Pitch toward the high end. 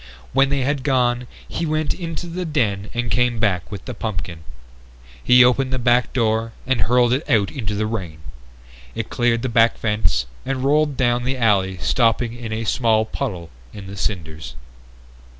No: low, 120 Hz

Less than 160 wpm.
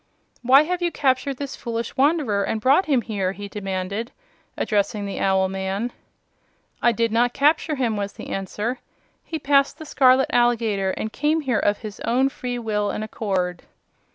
No: average, 170 wpm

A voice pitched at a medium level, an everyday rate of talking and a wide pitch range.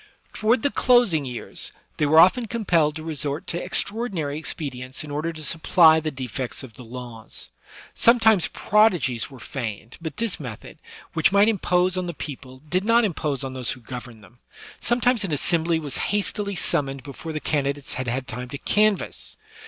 Yes: medium, 155 Hz; average, 175 wpm; wide, 6.7 semitones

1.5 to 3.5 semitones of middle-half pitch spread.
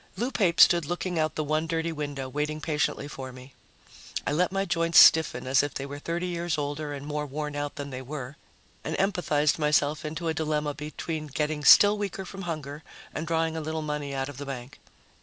Yes: narrow, 2.4 semitones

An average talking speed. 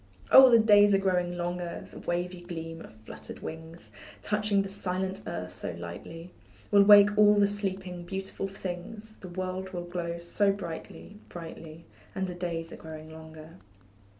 Yes: average, 160 wpm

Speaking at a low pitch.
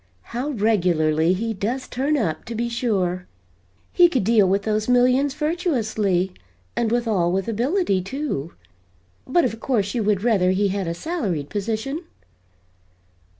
No: high, 220 Hz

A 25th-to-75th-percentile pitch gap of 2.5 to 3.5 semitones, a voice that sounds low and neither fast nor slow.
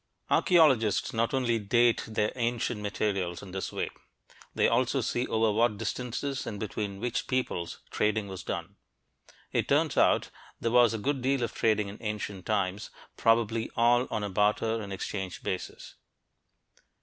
Yes: average, 2.8 semitones; low, 110 Hz; average, 160 wpm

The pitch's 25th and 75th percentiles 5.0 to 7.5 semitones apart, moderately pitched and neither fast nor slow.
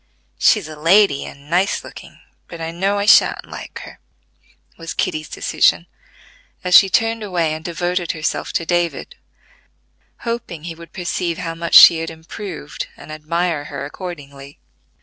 No: average, 2.7 semitones; medium, 170 Hz; average, 150 wpm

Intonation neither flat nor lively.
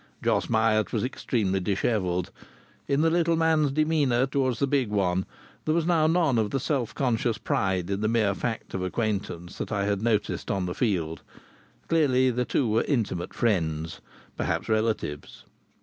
No: wide, 5.8 semitones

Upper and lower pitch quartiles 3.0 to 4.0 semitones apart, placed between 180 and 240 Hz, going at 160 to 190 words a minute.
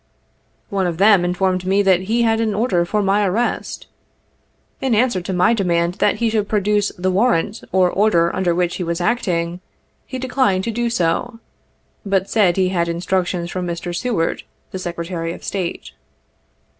Yes: average, 3.5 semitones; high, 190 Hz; average, 170 wpm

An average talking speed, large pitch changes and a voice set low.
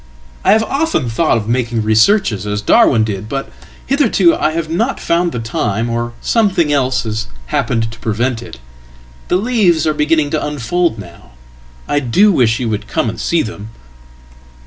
Yes: average, 160 wpm; wide, 7.2 semitones; low, 125 Hz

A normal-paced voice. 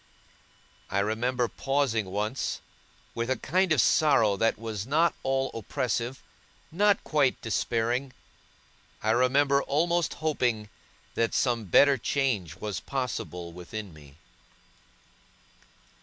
No: slow, 110 wpm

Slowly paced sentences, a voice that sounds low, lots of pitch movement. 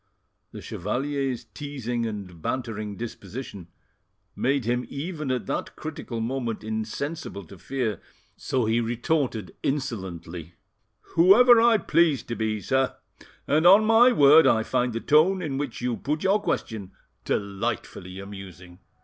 Yes: slow, 130 wpm; low, 120 Hz; wide, 5.7 semitones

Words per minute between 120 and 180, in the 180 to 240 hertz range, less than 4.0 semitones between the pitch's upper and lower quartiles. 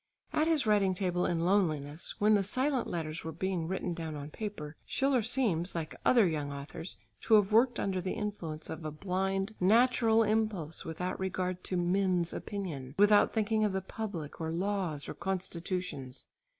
No: average, 170 wpm; medium, 185 Hz; average, 4.3 semitones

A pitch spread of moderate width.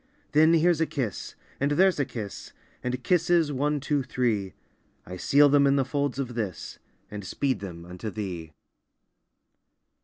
No: wide, 5.9 semitones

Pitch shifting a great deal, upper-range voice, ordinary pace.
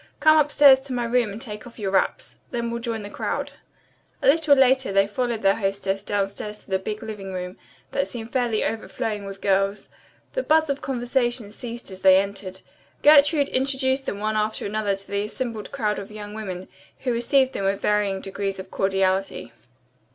No: average, 4.3 semitones; high, 215 Hz; average, 190 wpm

